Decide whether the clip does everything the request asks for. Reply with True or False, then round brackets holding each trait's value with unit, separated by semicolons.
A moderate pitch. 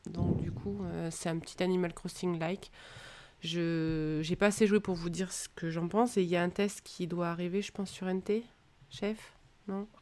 True (180 Hz)